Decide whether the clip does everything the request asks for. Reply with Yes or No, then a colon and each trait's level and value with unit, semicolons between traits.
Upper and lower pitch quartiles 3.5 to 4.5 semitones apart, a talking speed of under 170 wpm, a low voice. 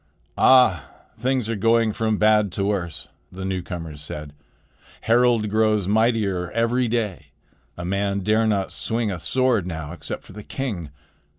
Yes: average, 4.0 semitones; average, 150 wpm; low, 105 Hz